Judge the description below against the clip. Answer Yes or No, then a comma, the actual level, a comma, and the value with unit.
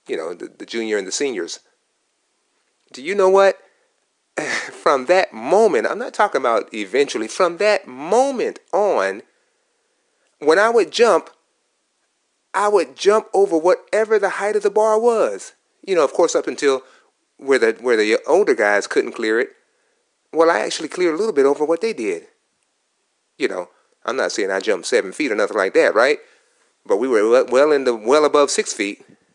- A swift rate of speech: No, average, 180 wpm